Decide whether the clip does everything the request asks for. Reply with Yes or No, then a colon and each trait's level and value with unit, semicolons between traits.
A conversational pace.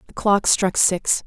Yes: average, 190 wpm